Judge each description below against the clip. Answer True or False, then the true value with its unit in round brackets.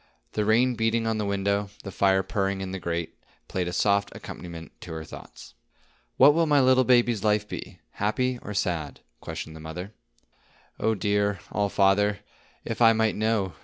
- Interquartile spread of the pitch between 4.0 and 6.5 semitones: False (2.7 semitones)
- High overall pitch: False (100 Hz)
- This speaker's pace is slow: False (170 wpm)